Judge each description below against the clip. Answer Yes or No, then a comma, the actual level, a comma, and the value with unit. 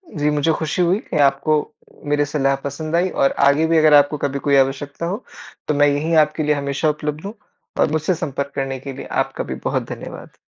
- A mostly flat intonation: Yes, narrow, 1.9 semitones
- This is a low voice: No, medium, 150 Hz